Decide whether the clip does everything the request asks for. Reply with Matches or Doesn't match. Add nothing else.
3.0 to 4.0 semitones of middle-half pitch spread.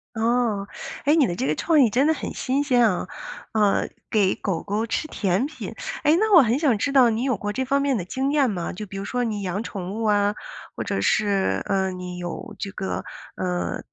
Doesn't match